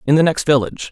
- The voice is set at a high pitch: No, medium, 145 Hz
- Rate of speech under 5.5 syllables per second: No, 7.8 syllables/s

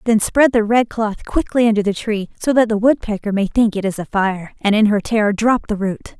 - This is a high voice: Yes, high, 215 Hz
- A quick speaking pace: Yes, fast, 250 wpm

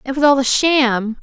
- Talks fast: Yes, fast, 245 wpm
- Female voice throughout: Yes, female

